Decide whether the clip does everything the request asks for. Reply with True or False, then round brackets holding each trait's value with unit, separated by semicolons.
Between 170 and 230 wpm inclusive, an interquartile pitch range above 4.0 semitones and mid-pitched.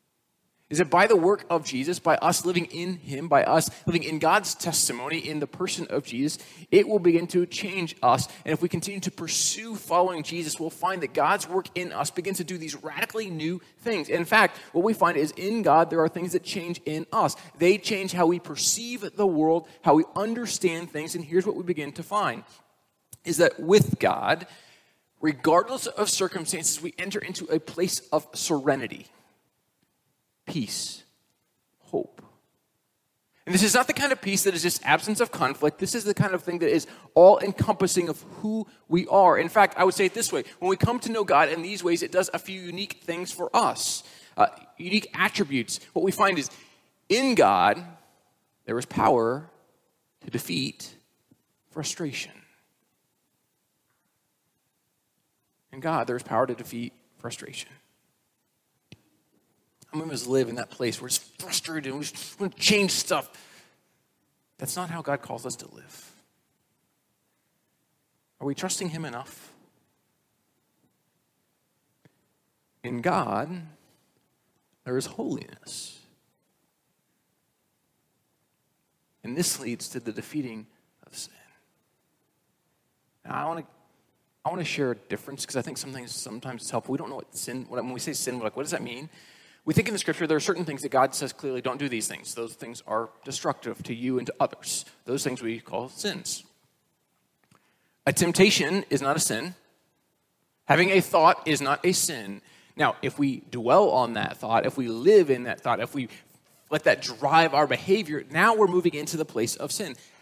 True (175 wpm; 5.1 semitones; 165 Hz)